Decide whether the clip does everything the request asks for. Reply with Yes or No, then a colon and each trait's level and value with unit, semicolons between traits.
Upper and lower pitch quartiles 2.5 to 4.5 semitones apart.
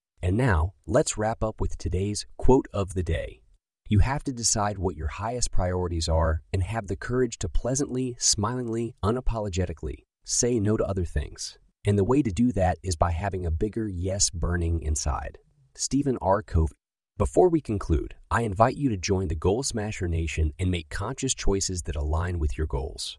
No: average, 5.2 semitones